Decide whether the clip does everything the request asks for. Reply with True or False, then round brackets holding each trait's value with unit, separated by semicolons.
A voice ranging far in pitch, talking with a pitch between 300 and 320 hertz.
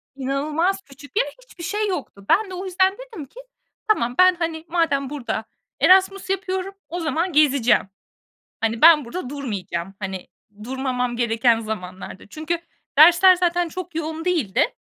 True (6.7 semitones; 315 Hz)